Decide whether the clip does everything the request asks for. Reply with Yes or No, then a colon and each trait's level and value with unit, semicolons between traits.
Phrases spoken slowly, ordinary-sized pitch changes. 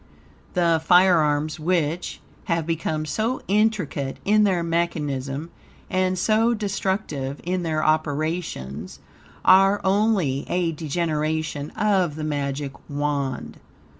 Yes: slow, 105 wpm; average, 4.0 semitones